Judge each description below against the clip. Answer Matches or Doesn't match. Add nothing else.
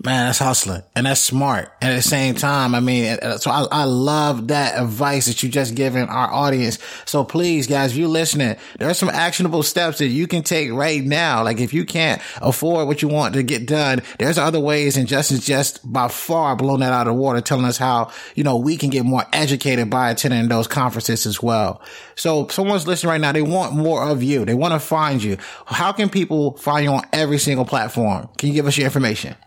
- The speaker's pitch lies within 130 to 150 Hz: Matches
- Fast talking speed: Matches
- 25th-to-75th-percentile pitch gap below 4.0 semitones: Matches